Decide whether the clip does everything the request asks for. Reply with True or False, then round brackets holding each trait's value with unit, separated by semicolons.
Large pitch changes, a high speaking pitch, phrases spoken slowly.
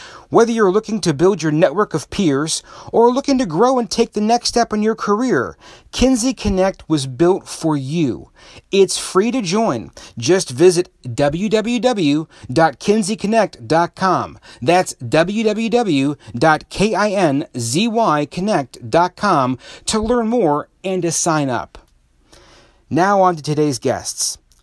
False (6.5 semitones; 180 Hz; 115 wpm)